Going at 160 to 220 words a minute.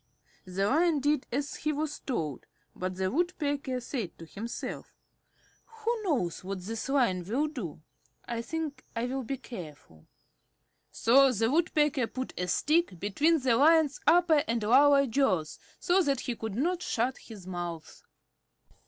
No: average, 150 wpm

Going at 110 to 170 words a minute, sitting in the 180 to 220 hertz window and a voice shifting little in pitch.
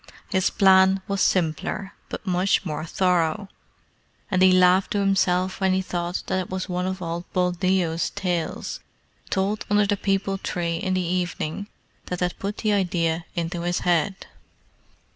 Yes: average, 160 wpm; medium, 185 Hz; narrow, 1.7 semitones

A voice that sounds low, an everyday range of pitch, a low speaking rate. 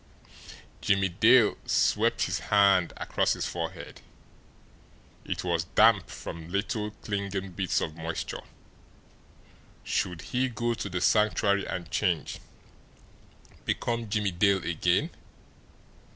Yes: low, 100 Hz; average, 3.5 semitones; slow, 110 wpm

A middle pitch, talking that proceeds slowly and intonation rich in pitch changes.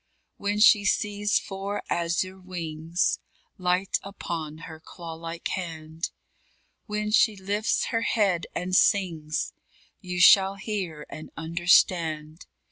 No: medium, 180 Hz; slow, 120 wpm; average, 3.5 semitones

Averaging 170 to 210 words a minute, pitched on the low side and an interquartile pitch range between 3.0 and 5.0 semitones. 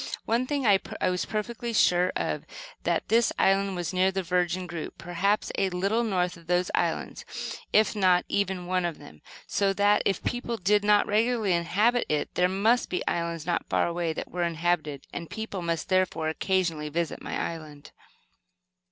No: average, 175 wpm; medium, 185 Hz; average, 3.3 semitones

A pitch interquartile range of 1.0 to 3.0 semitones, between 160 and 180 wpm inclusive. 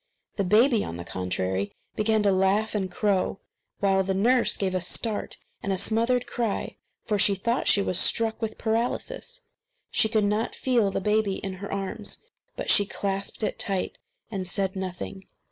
Yes: narrow, 2.6 semitones; average, 175 wpm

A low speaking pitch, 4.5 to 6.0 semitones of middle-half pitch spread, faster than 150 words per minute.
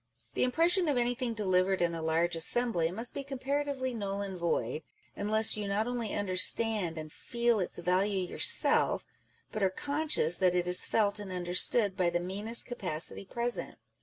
No: high, 200 Hz; average, 5.0 semitones; average, 170 wpm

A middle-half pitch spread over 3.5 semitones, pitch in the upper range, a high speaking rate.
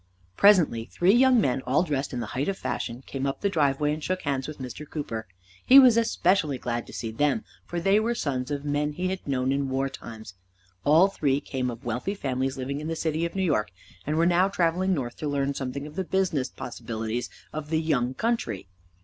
No: average, 5.3 semitones; medium, 145 Hz; fast, 220 wpm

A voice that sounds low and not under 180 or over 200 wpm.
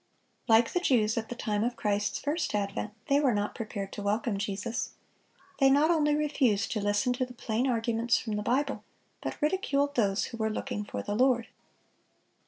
No: high, 230 Hz; average, 190 wpm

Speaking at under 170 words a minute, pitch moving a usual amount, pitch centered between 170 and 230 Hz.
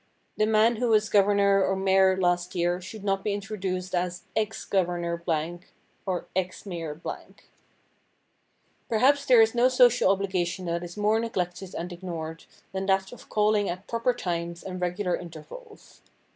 Yes: average, 155 wpm; average, 3.3 semitones; high, 190 Hz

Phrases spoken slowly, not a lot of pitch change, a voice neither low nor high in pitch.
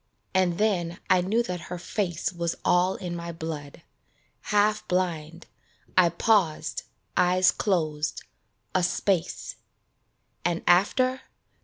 Yes: slow, 115 wpm; narrow, 2.2 semitones; medium, 180 Hz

